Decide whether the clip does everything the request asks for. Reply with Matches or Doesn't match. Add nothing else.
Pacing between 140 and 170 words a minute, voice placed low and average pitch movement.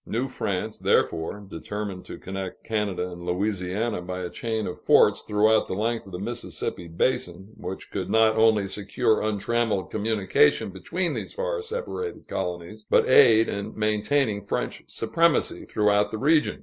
Matches